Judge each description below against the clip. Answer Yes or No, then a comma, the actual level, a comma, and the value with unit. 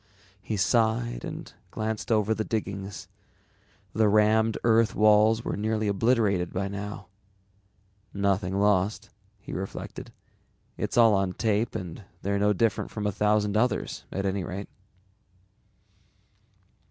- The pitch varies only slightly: Yes, narrow, 2.0 semitones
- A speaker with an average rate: No, slow, 130 wpm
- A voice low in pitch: Yes, low, 105 Hz